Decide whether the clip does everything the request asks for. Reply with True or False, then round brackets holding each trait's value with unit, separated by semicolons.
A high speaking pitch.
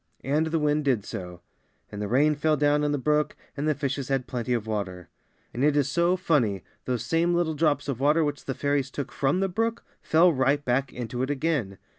False (145 Hz)